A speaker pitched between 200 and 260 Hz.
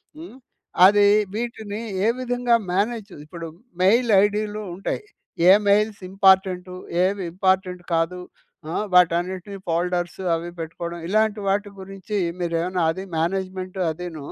No: high, 190 Hz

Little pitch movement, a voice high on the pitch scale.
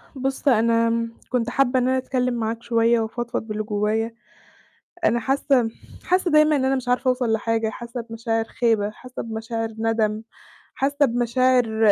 Yes: narrow, 2.2 semitones; high, 235 Hz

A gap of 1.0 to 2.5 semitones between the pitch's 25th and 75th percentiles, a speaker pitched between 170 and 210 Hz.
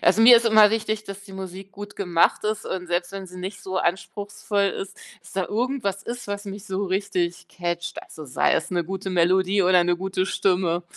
Yes: narrow, 2.2 semitones; high, 190 Hz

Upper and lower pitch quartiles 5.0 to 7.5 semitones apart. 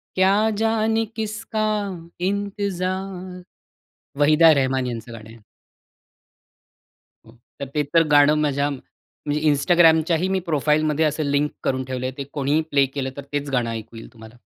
Yes: wide, 5.4 semitones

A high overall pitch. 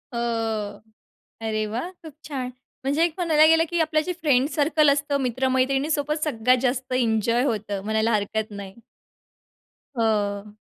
Yes: very high, 260 Hz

